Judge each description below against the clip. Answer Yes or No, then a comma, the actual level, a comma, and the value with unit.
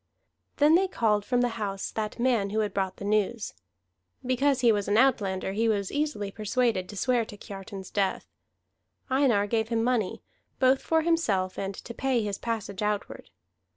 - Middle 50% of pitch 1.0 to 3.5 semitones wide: No, average, 3.9 semitones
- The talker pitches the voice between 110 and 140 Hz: No, high, 220 Hz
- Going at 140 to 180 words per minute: Yes, average, 175 wpm